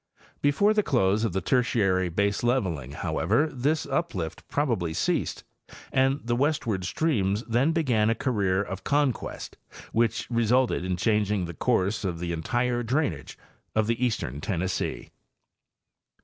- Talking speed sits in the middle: No, slow, 130 wpm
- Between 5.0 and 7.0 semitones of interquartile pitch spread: Yes, wide, 5.6 semitones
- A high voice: No, low, 115 Hz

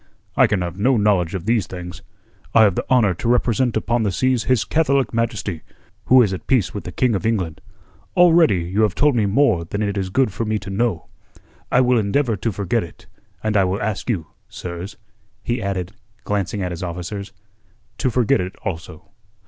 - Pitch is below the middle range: Yes, low, 105 Hz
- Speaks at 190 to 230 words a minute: Yes, average, 200 wpm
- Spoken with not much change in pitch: No, average, 4.5 semitones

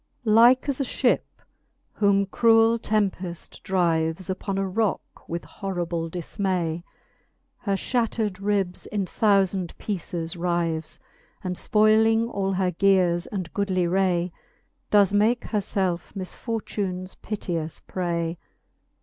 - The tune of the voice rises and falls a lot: No, average, 3.1 semitones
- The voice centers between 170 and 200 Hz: Yes, high, 190 Hz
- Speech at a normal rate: No, slow, 115 wpm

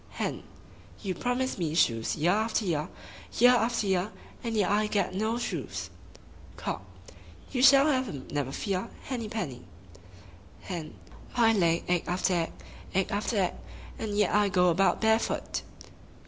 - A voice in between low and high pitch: No, high, 200 Hz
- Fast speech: No, average, 150 wpm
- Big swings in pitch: No, average, 4.2 semitones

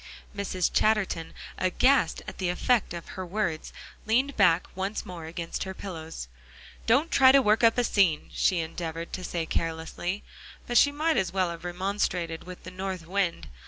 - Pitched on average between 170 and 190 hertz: Yes, medium, 185 Hz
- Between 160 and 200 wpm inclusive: Yes, average, 170 wpm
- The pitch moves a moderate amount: Yes, average, 4.0 semitones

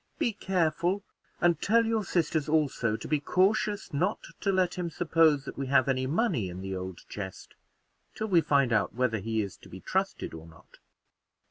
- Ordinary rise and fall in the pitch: No, wide, 8.5 semitones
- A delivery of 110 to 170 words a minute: No, average, 190 wpm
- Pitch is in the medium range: Yes, medium, 150 Hz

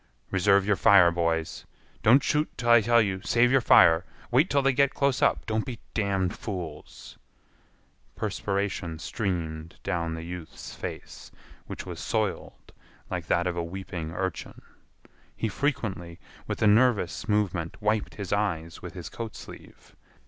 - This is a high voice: No, low, 100 Hz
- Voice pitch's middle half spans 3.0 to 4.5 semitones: No, average, 5.0 semitones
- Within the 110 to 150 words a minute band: Yes, average, 140 wpm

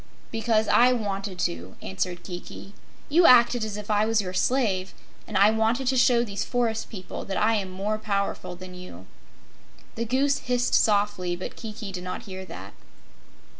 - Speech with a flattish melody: No, average, 3.8 semitones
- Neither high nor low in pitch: No, high, 210 Hz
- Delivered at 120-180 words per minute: Yes, average, 170 wpm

